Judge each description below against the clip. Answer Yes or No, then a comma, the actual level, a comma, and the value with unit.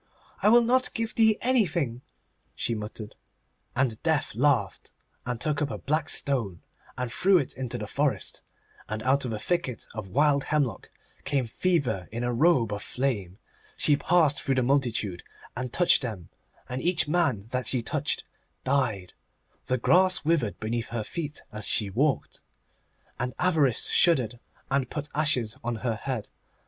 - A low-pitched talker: Yes, low, 130 Hz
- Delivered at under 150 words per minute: No, average, 160 wpm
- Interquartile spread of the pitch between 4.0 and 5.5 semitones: Yes, average, 5.1 semitones